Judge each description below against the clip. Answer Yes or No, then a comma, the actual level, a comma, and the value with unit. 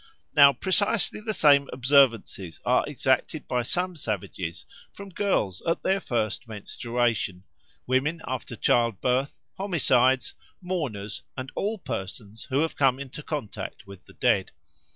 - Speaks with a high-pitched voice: No, low, 130 Hz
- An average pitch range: No, wide, 6.6 semitones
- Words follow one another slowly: Yes, slow, 130 wpm